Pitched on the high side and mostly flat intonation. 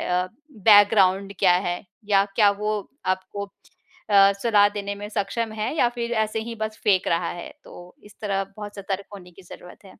Yes: high, 200 Hz; narrow, 1.9 semitones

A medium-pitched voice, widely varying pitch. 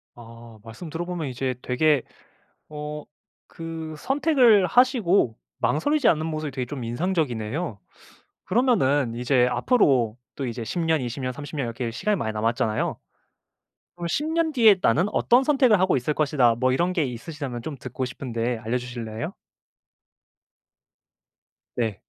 Yes: medium, 145 Hz; wide, 6.5 semitones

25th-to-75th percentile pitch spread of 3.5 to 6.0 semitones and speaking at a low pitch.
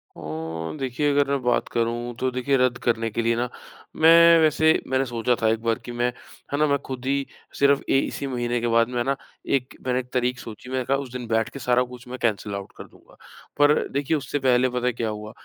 No: average, 2.8 semitones; low, 125 Hz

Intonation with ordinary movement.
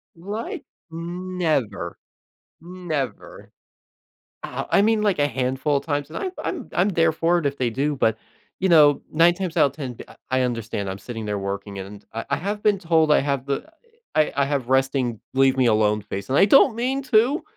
No: wide, 6.6 semitones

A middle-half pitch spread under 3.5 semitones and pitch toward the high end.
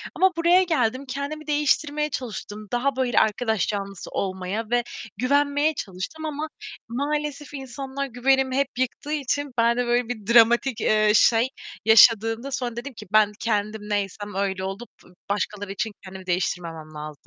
No: average, 5.1 semitones; high, 240 Hz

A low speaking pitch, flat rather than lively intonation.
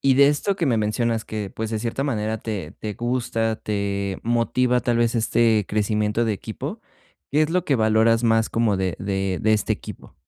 Yes: low, 110 Hz; narrow, 2.1 semitones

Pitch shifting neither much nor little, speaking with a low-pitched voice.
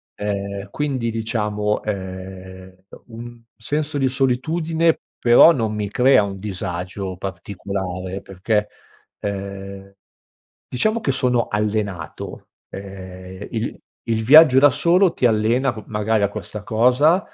Yes: average, 4.5 semitones; low, 105 Hz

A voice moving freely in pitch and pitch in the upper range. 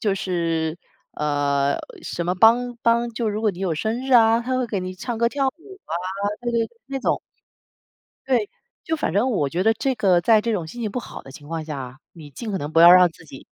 Yes: wide, 6.3 semitones; high, 200 Hz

